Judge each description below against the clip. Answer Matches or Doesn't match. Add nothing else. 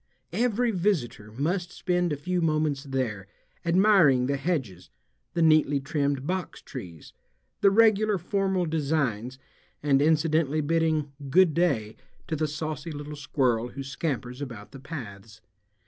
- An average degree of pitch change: Matches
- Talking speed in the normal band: Doesn't match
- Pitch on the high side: Doesn't match